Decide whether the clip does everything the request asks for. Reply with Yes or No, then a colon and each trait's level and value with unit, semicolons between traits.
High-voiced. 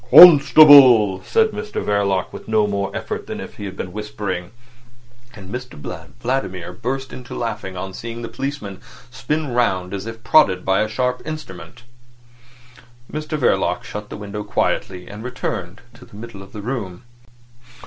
No: low, 105 Hz